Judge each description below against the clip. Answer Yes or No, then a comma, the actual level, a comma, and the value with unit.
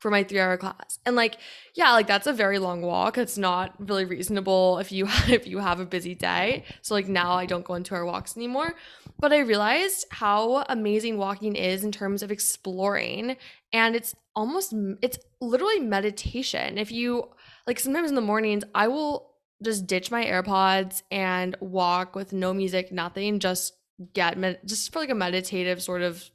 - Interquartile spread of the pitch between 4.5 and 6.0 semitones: No, average, 3.7 semitones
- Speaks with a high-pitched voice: Yes, high, 200 Hz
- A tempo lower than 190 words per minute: Yes, average, 180 wpm